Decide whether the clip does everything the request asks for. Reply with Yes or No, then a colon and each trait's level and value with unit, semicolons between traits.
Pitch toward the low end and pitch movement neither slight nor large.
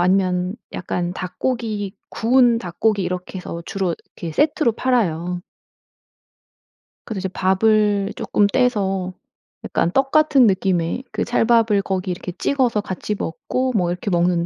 No: high, 195 Hz; average, 4.2 semitones